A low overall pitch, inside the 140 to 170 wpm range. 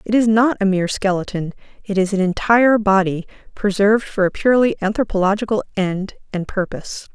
No: high, 200 Hz; average, 160 wpm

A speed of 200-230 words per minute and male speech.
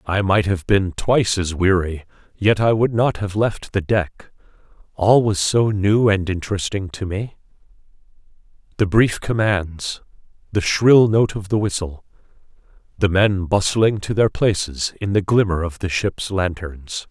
No: average, 155 wpm; male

